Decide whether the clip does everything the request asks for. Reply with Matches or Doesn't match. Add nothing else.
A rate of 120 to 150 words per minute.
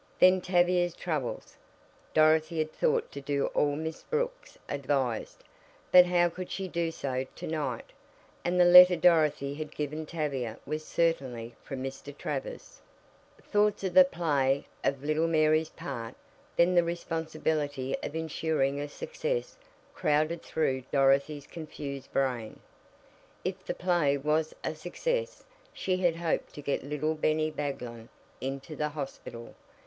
Matches